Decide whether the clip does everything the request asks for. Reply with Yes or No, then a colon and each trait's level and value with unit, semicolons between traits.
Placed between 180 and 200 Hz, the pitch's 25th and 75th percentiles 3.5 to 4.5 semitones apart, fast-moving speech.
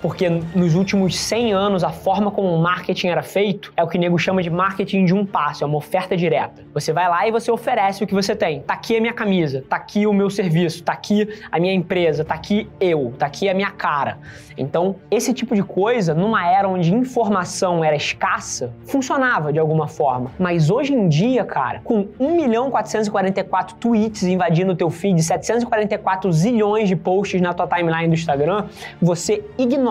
Yes: high, 190 Hz; average, 3.8 semitones; fast, 200 wpm